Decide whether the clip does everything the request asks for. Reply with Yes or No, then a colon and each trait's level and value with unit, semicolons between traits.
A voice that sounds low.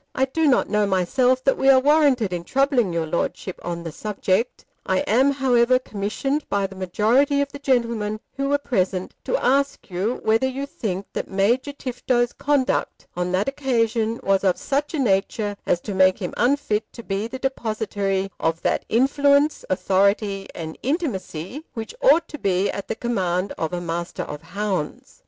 No: high, 220 Hz